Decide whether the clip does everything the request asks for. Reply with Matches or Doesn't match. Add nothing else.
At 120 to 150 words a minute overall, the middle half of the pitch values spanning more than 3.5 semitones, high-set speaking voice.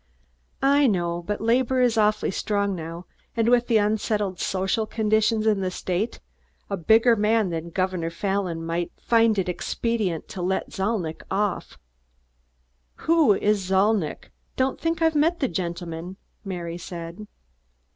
Matches